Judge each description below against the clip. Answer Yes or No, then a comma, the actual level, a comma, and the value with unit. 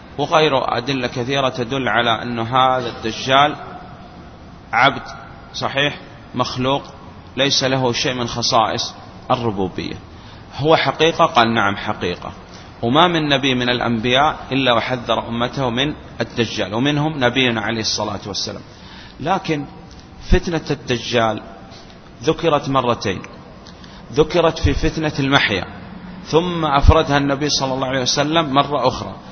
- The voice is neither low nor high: No, low, 130 Hz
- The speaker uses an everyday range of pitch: Yes, average, 4.1 semitones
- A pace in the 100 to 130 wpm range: Yes, average, 115 wpm